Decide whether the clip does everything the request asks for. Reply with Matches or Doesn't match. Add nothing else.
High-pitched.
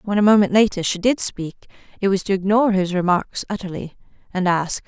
Matches